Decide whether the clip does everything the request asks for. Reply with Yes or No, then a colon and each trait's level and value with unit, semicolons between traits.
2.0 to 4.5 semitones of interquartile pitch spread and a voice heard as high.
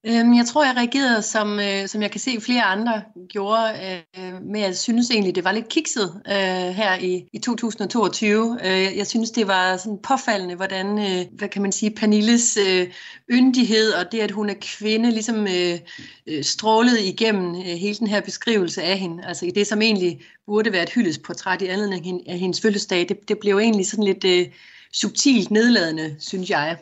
Yes: average, 3.2 semitones; high, 205 Hz